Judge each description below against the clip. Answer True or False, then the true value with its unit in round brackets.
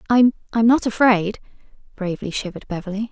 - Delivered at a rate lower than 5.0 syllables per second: False (6.5 syllables/s)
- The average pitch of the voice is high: True (210 Hz)